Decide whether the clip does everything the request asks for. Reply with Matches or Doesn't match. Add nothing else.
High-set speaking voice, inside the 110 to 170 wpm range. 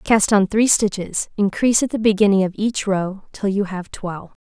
Doesn't match